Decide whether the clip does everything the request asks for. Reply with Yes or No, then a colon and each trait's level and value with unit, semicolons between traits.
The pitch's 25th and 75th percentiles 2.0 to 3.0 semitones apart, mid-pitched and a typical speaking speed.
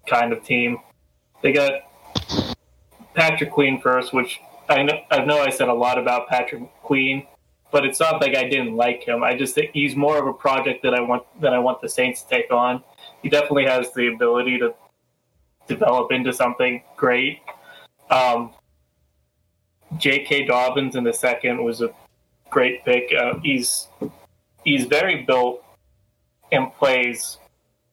No: narrow, 2.5 semitones; low, 125 Hz; average, 160 wpm